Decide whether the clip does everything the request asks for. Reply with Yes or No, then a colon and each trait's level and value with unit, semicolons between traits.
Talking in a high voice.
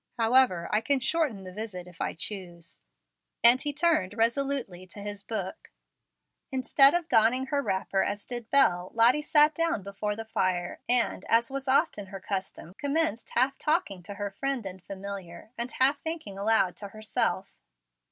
Yes: high, 225 Hz